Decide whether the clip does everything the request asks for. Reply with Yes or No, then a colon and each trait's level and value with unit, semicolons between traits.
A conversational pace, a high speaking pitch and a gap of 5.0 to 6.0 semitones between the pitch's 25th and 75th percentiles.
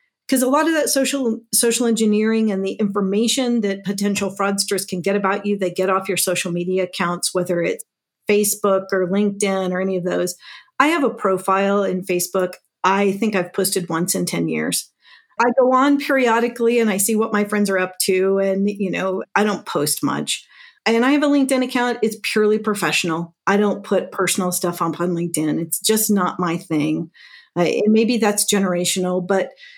No: average, 195 wpm; high, 200 Hz; average, 3.3 semitones